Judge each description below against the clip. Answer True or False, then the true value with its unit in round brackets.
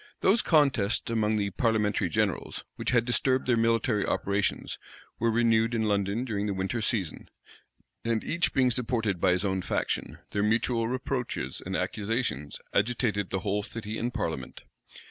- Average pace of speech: True (155 wpm)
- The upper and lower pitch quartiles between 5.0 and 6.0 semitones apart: False (3.0 semitones)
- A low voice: True (110 Hz)